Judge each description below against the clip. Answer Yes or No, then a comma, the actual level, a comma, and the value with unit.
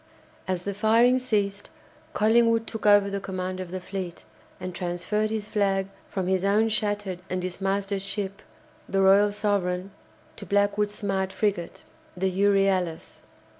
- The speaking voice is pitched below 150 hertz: No, high, 200 Hz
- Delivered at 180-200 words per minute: No, average, 140 wpm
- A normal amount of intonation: No, narrow, 1.9 semitones